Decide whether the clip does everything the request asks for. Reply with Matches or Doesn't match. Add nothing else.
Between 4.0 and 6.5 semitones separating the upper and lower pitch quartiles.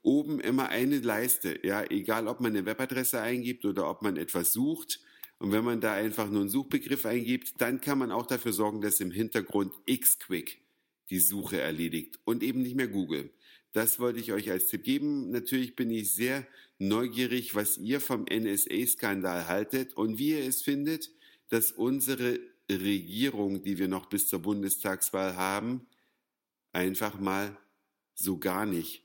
Matches